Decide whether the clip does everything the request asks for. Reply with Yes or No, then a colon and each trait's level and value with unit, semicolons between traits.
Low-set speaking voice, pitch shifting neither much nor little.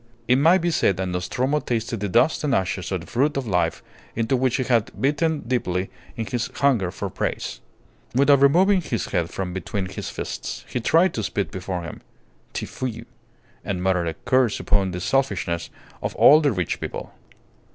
No: low, 115 Hz; wide, 6.7 semitones